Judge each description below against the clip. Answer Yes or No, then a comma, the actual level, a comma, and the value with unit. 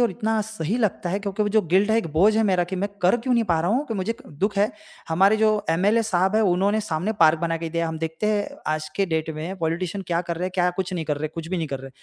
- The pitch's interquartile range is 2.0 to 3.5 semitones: No, average, 4.3 semitones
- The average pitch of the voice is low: No, medium, 185 Hz